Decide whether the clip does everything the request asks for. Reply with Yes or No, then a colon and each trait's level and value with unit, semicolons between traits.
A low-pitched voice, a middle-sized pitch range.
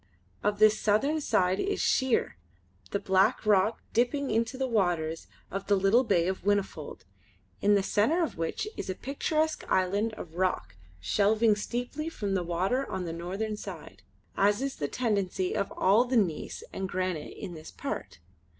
No: high, 205 Hz; average, 4.2 semitones